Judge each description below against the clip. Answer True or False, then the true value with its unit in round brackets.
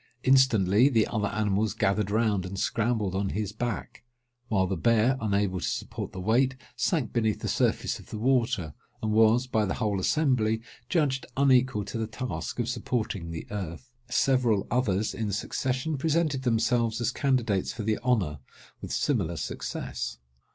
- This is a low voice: True (110 Hz)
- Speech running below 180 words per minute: True (160 wpm)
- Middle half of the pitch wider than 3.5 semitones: True (3.9 semitones)